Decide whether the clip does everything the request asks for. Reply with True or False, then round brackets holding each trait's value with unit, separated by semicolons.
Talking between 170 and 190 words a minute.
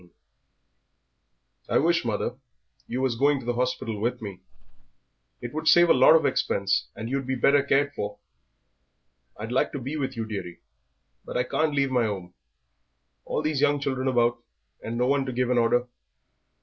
True (180 wpm)